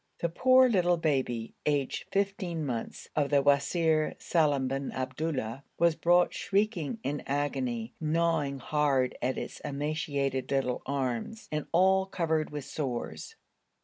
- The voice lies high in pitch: No, medium, 150 Hz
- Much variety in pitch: No, average, 3.8 semitones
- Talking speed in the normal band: No, slow, 130 wpm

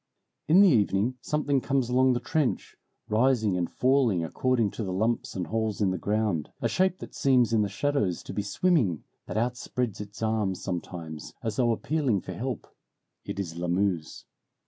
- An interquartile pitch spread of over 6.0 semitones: No, average, 4.9 semitones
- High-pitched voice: No, low, 110 Hz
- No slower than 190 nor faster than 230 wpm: No, average, 175 wpm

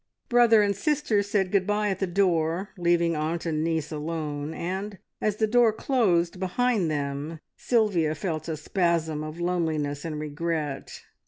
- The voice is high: No, medium, 170 Hz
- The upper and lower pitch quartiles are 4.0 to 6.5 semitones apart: Yes, average, 4.4 semitones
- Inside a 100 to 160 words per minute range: Yes, average, 155 wpm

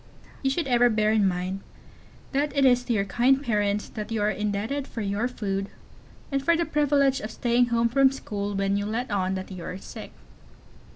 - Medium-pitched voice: No, high, 225 Hz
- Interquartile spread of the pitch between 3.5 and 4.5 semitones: No, average, 4.9 semitones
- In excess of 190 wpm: Yes, fast, 205 wpm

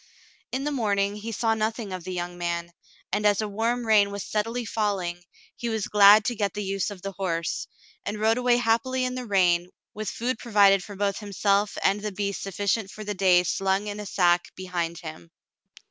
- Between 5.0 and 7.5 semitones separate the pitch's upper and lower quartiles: No, average, 2.7 semitones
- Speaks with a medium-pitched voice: No, high, 205 Hz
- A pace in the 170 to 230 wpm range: Yes, fast, 205 wpm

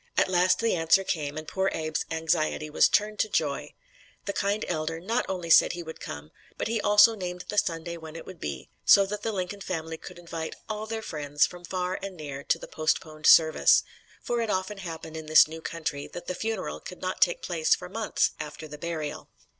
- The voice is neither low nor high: Yes, medium, 170 Hz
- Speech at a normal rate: No, fast, 215 wpm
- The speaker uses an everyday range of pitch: Yes, average, 3.6 semitones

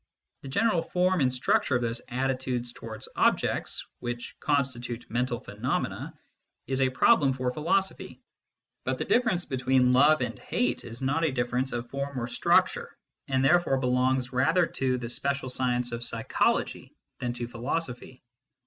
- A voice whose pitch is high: No, low, 130 Hz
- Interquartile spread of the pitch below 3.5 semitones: Yes, narrow, 2.4 semitones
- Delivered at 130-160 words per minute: Yes, average, 150 wpm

